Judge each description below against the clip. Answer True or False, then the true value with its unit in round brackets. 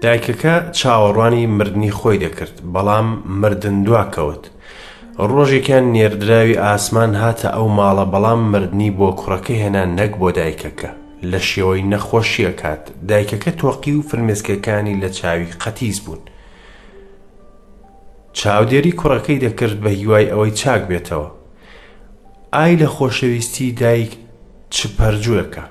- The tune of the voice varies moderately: True (3.1 semitones)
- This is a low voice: True (105 Hz)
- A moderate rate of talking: False (110 wpm)